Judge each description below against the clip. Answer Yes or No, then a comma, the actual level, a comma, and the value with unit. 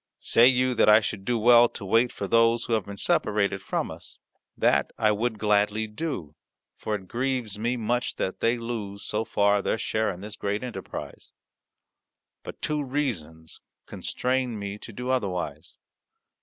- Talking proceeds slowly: No, average, 170 wpm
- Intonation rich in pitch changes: No, average, 3.2 semitones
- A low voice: Yes, low, 110 Hz